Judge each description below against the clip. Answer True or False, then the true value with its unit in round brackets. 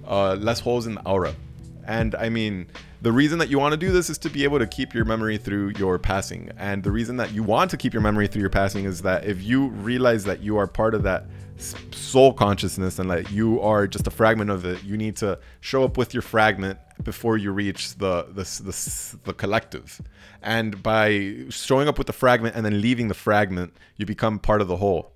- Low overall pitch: True (105 Hz)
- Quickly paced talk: True (230 wpm)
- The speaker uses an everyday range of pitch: True (3.2 semitones)